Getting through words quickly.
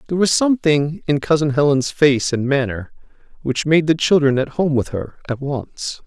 No: average, 190 wpm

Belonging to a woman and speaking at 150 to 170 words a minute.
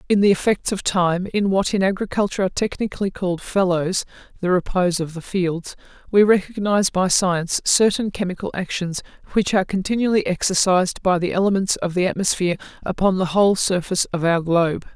Yes: female; average, 160 wpm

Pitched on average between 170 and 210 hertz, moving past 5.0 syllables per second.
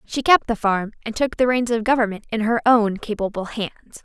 No: high, 225 Hz; 5.5 syllables/s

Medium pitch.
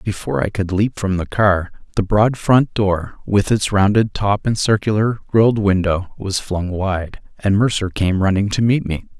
No: low, 100 Hz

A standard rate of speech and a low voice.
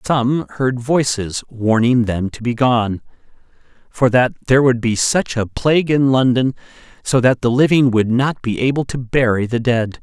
Yes: average, 180 wpm; low, 125 Hz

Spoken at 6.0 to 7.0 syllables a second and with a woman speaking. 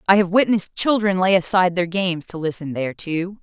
Yes: 6.1 syllables/s; female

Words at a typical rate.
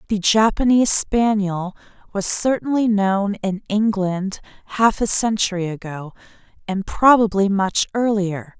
No: slow, 110 wpm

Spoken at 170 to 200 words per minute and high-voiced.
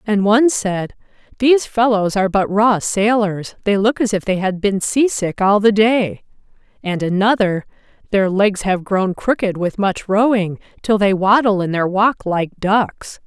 Yes: average, 175 wpm; high, 205 Hz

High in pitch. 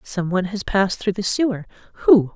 Yes: high, 195 Hz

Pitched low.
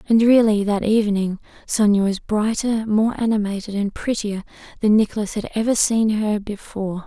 No: high, 210 Hz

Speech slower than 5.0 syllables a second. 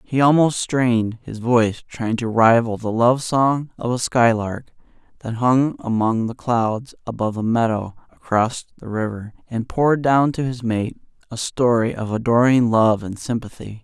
Yes: 4.5 syllables/s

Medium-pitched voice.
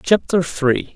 Yes: medium, 145 Hz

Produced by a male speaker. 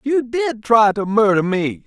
Yes: male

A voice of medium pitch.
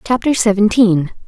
No: high, 210 Hz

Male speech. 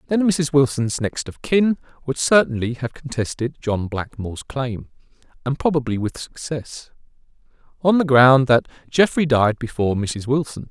Yes: male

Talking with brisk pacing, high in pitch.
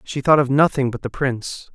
No: fast, 240 wpm; low, 135 Hz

